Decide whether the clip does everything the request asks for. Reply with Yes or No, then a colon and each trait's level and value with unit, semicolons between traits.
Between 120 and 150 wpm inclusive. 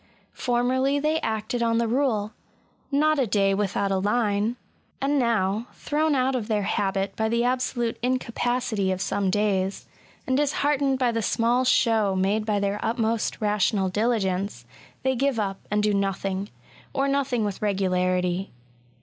No: average, 160 wpm